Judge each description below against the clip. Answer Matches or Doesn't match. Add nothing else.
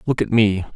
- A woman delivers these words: Doesn't match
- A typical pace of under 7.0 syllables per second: Matches